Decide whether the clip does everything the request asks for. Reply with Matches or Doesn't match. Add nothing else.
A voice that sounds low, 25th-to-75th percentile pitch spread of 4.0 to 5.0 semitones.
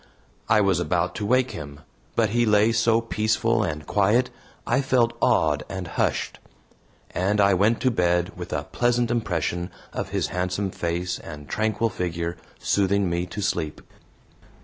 Matches